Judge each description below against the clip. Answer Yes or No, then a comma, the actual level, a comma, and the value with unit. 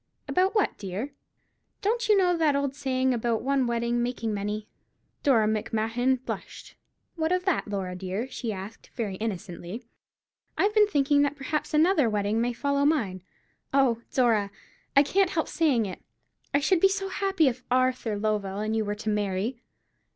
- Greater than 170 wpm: No, average, 165 wpm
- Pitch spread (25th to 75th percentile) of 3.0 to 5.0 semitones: No, wide, 5.5 semitones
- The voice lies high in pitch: Yes, high, 245 Hz